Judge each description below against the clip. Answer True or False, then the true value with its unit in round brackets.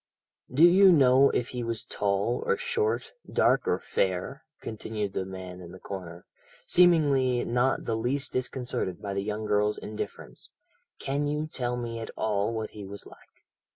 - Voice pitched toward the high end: False (115 Hz)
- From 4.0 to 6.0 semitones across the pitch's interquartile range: True (5.2 semitones)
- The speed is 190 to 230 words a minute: False (165 wpm)